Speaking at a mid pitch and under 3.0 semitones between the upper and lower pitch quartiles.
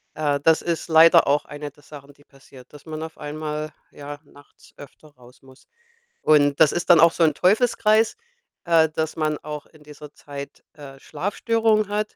Yes: medium, 155 Hz; narrow, 2.6 semitones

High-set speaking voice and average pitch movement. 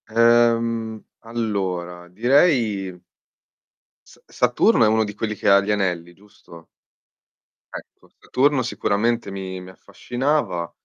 No: low, 110 Hz; average, 4.0 semitones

